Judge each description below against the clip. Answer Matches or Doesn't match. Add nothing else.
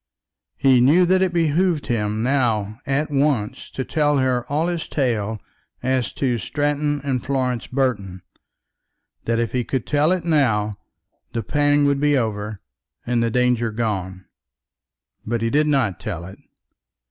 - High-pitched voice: Doesn't match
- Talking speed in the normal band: Matches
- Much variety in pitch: Doesn't match